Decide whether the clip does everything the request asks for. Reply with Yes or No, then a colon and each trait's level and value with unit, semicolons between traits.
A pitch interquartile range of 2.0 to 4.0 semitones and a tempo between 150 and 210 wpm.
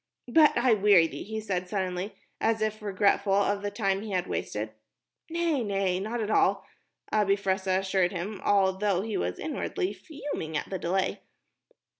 Yes: narrow, 2.5 semitones; average, 165 wpm